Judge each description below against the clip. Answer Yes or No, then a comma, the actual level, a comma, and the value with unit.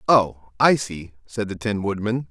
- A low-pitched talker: Yes, low, 105 Hz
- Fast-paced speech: No, average, 180 wpm